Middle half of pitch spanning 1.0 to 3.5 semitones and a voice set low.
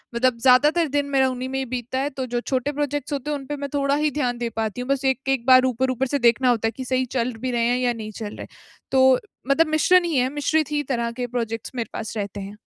No: average, 2.7 semitones; very high, 260 Hz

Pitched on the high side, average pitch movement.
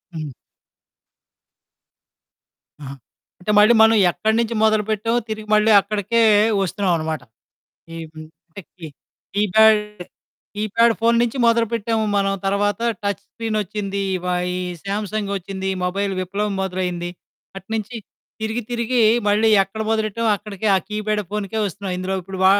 No: high, 205 Hz; narrow, 2.3 semitones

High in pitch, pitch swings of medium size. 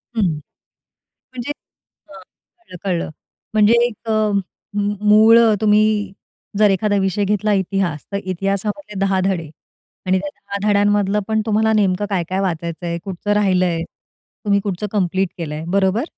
No: high, 200 Hz; narrow, 2.2 semitones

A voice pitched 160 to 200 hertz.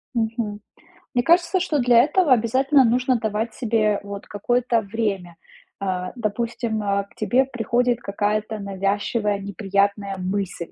No: high, 220 Hz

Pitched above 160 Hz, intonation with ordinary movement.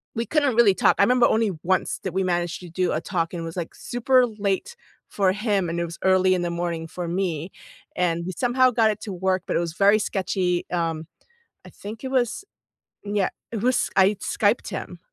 Yes: high, 190 Hz; average, 4.0 semitones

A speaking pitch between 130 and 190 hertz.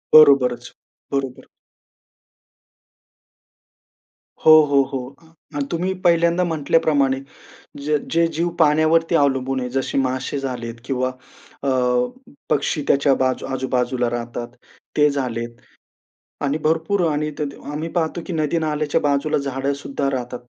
Yes: medium, 140 Hz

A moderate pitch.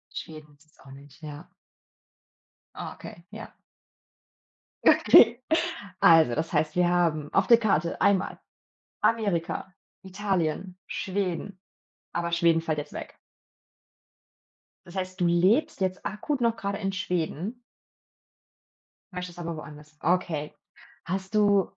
Yes: medium, 180 Hz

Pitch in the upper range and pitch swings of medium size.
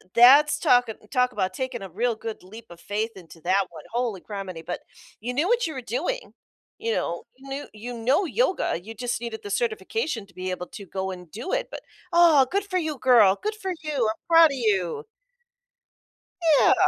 No: high, 235 Hz; wide, 6.8 semitones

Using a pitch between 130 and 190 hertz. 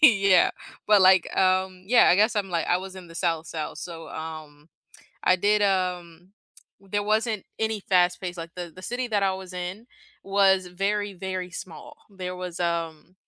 Yes: medium, 185 Hz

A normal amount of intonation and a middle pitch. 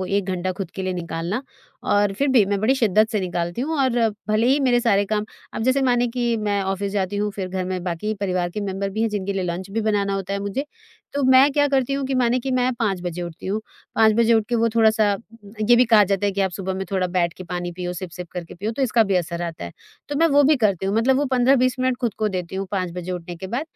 No: average, 4.5 semitones; high, 205 Hz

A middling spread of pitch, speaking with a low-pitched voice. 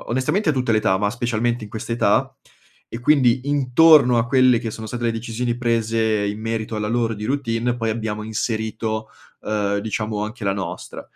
No: narrow, 2.1 semitones; low, 115 Hz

